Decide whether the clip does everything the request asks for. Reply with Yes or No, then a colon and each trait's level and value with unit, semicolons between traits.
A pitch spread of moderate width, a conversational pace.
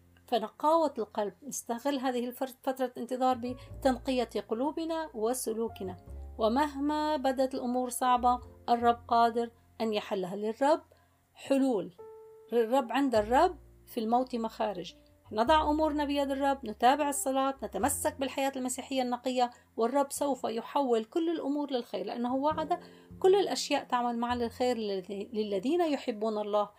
Yes: average, 3.7 semitones; average, 120 wpm